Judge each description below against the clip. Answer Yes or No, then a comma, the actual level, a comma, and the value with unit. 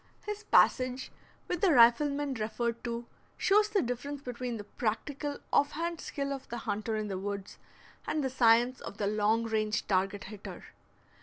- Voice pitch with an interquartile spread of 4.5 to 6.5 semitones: Yes, average, 4.8 semitones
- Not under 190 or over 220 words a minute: No, average, 165 wpm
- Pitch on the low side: No, high, 240 Hz